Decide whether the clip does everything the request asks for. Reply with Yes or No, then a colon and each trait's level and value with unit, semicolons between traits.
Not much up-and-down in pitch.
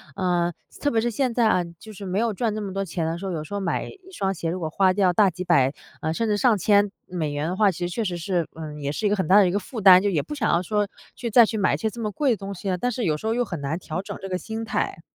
No: average, 3.9 semitones